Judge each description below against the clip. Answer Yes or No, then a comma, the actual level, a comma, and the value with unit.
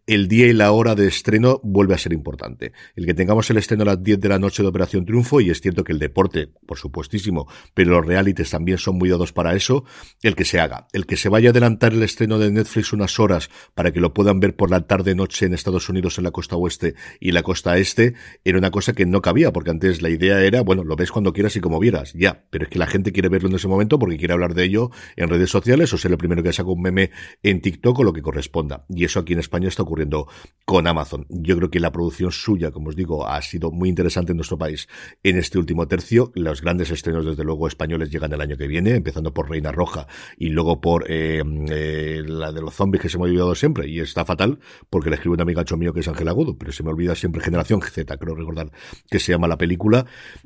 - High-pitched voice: No, very low, 90 Hz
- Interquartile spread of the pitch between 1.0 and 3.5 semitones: Yes, average, 3.2 semitones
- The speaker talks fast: Yes, fast, 255 wpm